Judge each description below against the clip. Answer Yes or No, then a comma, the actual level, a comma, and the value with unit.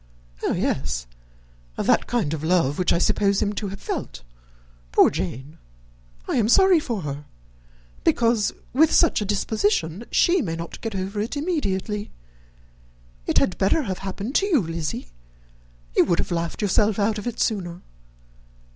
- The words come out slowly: No, average, 155 wpm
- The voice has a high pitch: Yes, high, 200 Hz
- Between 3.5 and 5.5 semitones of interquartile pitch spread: Yes, average, 5.2 semitones